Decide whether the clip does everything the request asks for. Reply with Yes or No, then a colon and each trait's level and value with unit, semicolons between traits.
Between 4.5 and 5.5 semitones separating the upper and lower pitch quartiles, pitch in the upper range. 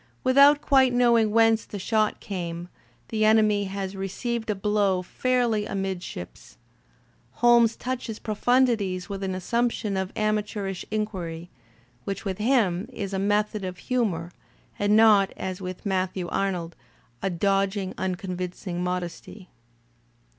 No: average, 3.1 semitones; high, 200 Hz